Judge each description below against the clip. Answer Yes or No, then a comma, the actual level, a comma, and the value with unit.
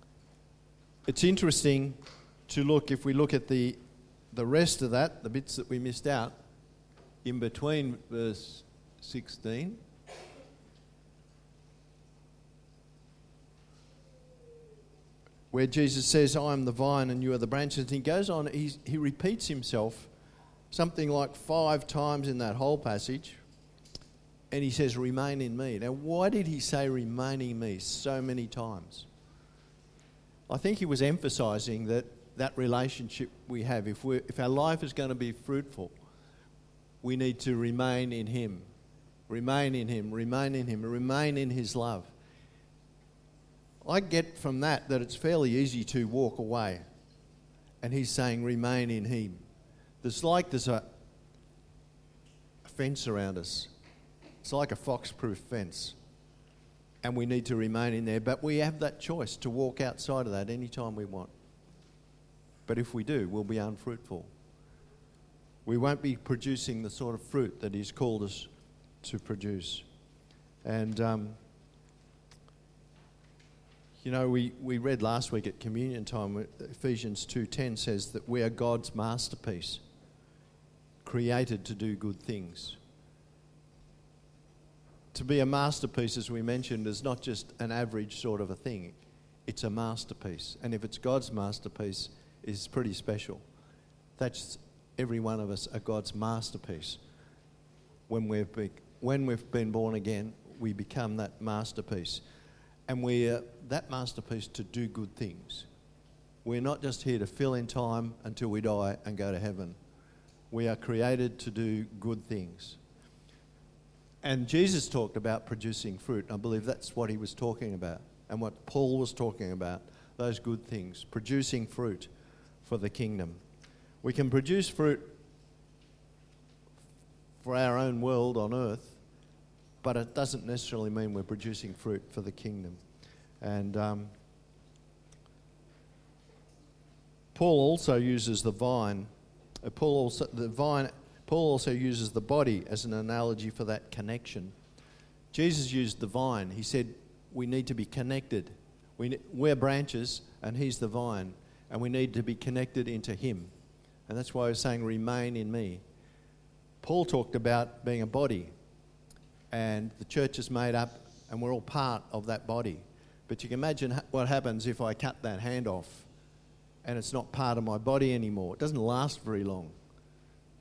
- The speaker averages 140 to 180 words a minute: Yes, average, 150 wpm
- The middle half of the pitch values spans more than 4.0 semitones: No, average, 3.6 semitones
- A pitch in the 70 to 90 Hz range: No, low, 120 Hz